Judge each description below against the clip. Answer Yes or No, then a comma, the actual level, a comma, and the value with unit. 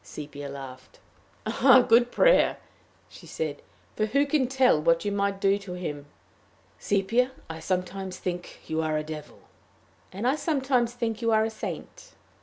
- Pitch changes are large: Yes, wide, 7.3 semitones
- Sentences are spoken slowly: No, average, 160 wpm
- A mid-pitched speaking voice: No, high, 200 Hz